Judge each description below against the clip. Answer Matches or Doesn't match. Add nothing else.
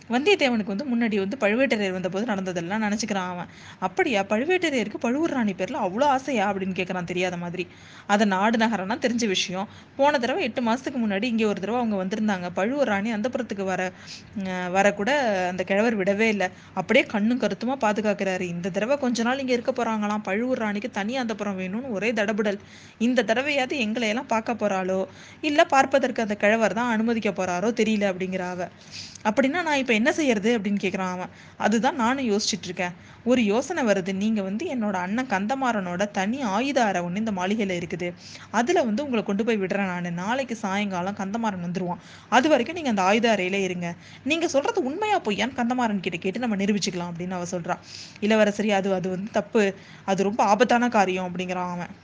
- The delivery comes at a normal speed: Doesn't match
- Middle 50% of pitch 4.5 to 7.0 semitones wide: Doesn't match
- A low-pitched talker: Doesn't match